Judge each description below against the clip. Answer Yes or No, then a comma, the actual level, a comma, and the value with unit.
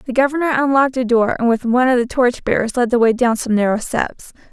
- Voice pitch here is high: Yes, high, 245 Hz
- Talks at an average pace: No, fast, 250 wpm